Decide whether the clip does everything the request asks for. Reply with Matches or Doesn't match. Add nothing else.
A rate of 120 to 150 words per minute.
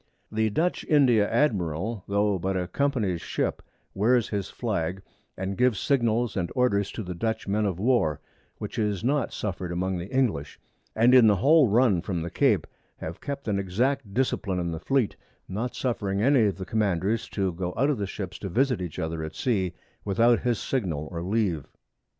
Doesn't match